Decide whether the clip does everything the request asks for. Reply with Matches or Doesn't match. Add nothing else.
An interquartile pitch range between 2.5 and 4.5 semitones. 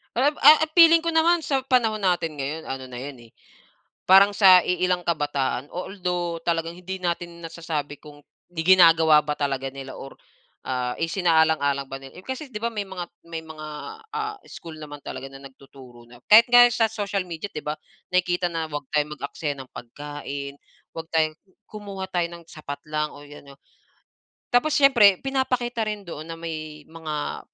Doesn't match